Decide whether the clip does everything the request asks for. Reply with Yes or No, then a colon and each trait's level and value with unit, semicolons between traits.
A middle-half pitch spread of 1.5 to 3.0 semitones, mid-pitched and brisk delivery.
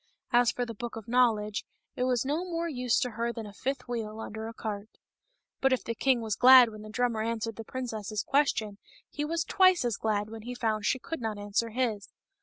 No: average, 2.7 semitones; high, 230 Hz; fast, 220 wpm